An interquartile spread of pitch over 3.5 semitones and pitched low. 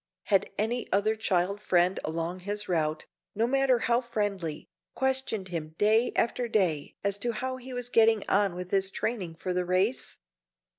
No: average, 4.5 semitones; high, 205 Hz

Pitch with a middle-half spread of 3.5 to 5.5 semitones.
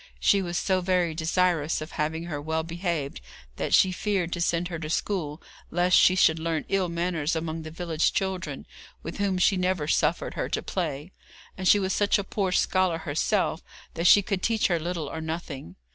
No: average, 2.7 semitones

